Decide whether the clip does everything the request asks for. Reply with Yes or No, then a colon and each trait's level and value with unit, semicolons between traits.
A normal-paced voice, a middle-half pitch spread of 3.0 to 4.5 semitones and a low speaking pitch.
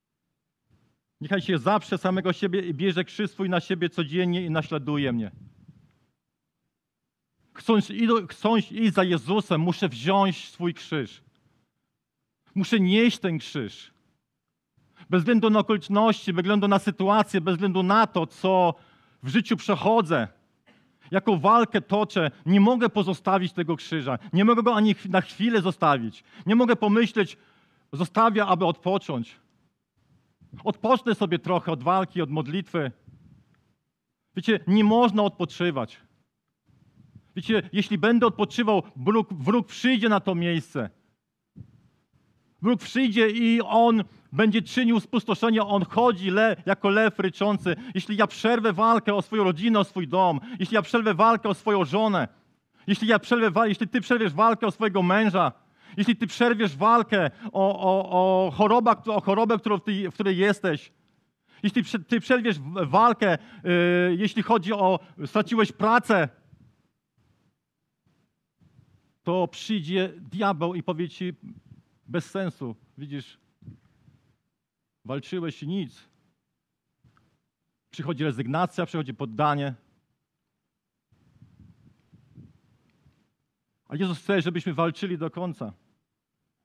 No: average, 120 wpm; average, 3.9 semitones; high, 195 Hz